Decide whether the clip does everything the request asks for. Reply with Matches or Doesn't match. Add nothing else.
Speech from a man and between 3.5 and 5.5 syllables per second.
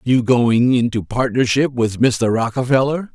Matches